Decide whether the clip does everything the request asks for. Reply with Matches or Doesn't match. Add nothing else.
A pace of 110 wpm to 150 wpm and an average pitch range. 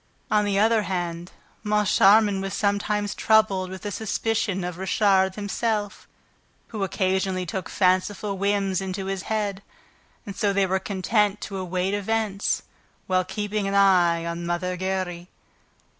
Doesn't match